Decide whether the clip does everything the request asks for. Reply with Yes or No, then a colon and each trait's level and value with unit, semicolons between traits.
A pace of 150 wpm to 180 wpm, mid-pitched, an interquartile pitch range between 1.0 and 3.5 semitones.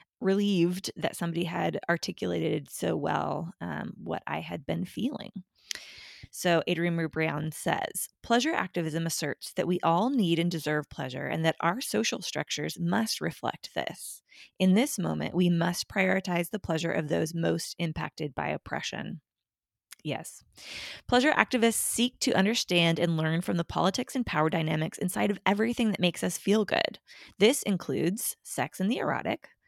No: average, 155 wpm; medium, 175 Hz; average, 3.9 semitones